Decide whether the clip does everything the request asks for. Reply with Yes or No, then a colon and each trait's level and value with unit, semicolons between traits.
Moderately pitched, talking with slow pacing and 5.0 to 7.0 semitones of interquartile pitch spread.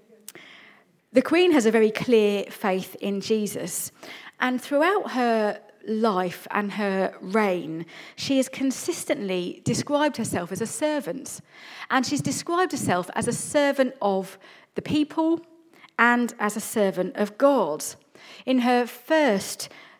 No: high, 230 Hz; slow, 130 wpm; wide, 5.6 semitones